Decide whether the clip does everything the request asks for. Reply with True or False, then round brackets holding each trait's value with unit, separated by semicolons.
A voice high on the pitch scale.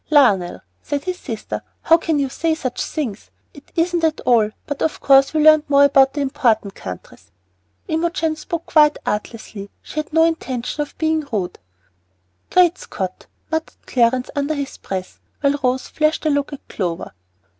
True (285 Hz)